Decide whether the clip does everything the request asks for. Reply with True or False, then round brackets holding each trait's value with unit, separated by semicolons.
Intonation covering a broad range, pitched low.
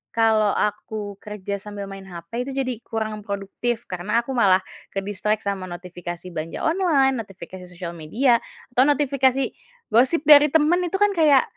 False (5.7 semitones; 215 Hz)